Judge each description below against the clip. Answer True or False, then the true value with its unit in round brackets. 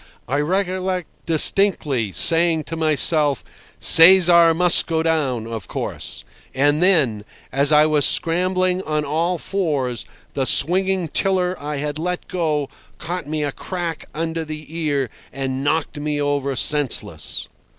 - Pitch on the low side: False (155 Hz)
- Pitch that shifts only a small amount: False (3.5 semitones)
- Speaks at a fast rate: False (135 wpm)